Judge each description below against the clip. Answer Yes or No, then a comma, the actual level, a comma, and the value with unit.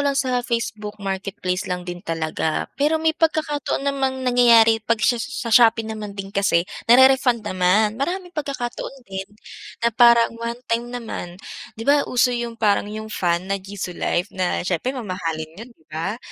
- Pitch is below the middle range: No, high, 225 Hz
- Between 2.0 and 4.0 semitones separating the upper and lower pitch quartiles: No, average, 4.5 semitones